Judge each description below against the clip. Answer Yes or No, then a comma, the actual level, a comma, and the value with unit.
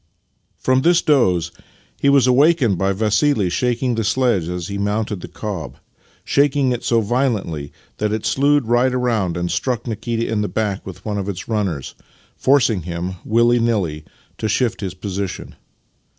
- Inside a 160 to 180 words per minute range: Yes, average, 165 wpm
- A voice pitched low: Yes, low, 110 Hz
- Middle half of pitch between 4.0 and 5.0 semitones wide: Yes, average, 4.6 semitones